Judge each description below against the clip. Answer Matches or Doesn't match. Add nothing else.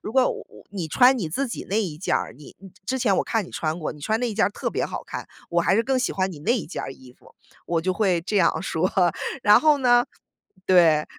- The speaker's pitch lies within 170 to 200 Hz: Matches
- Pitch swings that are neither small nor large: Doesn't match